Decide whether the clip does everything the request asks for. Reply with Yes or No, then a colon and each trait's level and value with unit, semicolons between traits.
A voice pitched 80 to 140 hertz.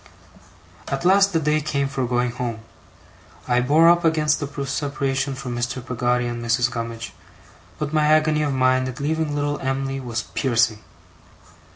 Yes: low, 135 Hz